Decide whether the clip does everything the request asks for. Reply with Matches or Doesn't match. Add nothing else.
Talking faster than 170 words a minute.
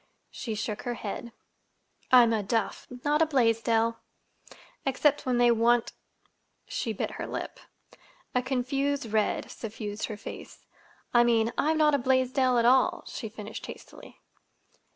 Doesn't match